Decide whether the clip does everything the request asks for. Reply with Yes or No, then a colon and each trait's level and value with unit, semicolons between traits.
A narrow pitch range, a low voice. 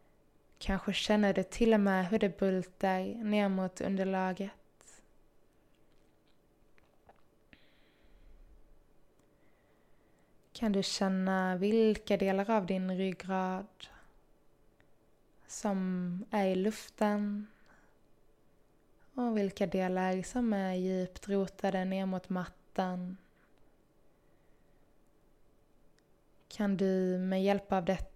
No: narrow, 1.5 semitones; high, 195 Hz